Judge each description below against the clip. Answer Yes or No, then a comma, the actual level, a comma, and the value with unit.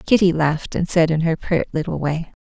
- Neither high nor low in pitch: Yes, medium, 165 Hz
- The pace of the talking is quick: Yes, fast, 225 wpm